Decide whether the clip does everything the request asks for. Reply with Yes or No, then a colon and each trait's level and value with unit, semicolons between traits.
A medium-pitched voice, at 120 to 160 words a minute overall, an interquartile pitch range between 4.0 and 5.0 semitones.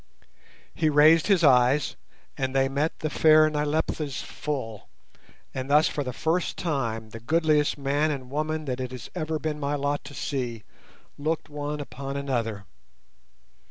No: medium, 145 Hz; average, 155 wpm; average, 2.9 semitones